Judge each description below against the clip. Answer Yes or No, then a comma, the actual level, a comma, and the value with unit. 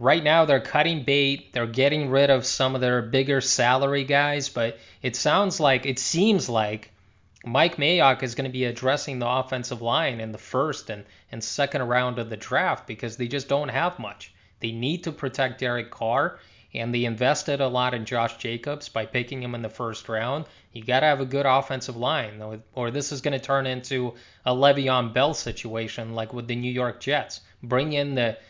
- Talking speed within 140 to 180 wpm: No, fast, 205 wpm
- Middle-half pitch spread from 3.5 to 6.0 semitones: No, average, 3.1 semitones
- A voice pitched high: No, low, 130 Hz